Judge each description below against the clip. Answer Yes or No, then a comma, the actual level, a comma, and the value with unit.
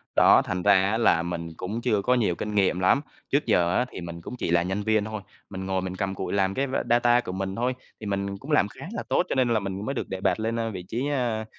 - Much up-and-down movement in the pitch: No, average, 3.8 semitones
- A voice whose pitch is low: Yes, low, 100 Hz